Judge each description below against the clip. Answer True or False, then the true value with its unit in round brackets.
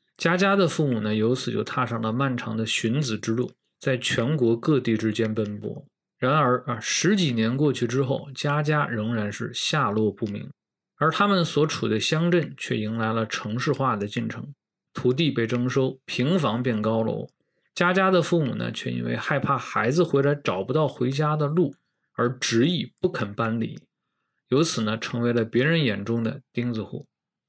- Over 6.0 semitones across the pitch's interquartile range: False (5.1 semitones)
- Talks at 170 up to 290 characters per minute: True (260 characters per minute)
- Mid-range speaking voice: False (125 Hz)